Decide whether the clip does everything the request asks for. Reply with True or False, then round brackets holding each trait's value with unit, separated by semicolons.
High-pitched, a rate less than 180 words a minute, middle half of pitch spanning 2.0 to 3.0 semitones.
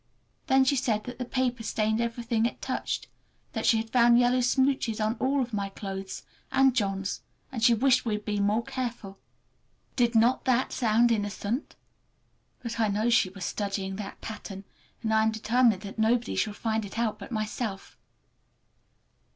True (225 Hz; 170 wpm; 2.6 semitones)